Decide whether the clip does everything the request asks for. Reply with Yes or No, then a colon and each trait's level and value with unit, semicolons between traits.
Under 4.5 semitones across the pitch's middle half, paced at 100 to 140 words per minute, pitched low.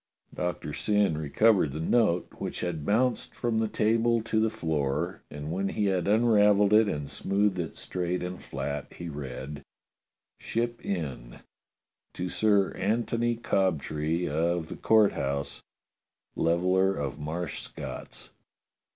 No: wide, 5.6 semitones; slow, 135 wpm; very low, 90 Hz